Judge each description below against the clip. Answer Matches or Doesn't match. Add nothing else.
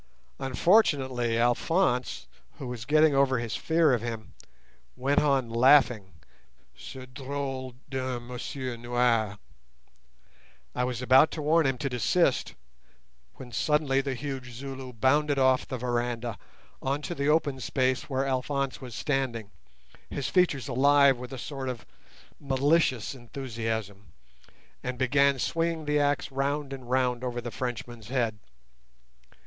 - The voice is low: Matches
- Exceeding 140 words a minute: Doesn't match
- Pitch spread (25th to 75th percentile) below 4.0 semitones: Matches